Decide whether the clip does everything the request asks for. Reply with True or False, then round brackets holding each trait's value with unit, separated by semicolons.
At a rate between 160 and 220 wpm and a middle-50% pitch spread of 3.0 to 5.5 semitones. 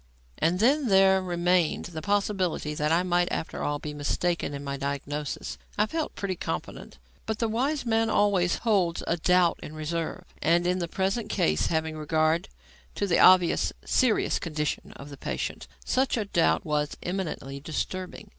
True (165 wpm; 4.6 semitones)